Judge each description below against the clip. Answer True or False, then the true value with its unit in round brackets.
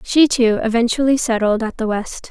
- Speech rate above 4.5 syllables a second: True (5.1 syllables/s)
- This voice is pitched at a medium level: False (235 Hz)